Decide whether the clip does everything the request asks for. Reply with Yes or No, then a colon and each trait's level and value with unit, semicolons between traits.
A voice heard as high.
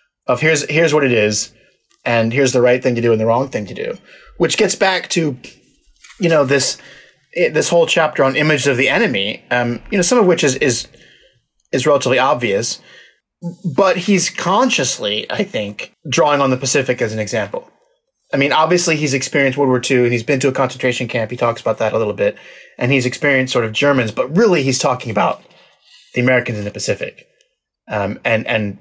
No: medium, 140 Hz